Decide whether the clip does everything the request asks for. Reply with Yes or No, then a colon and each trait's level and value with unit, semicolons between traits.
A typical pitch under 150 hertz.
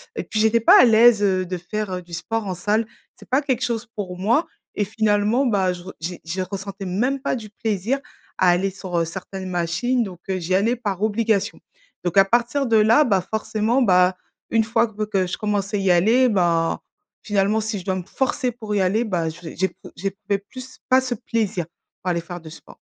No: high, 205 Hz